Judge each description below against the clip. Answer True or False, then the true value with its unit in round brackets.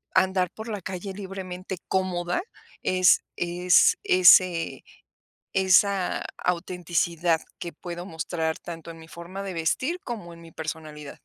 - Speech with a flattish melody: True (2.0 semitones)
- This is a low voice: False (180 Hz)